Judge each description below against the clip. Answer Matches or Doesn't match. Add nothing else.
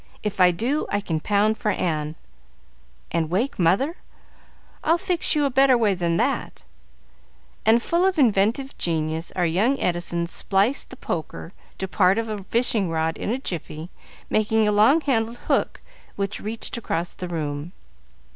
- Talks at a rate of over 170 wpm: Doesn't match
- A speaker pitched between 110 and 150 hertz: Doesn't match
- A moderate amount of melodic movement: Doesn't match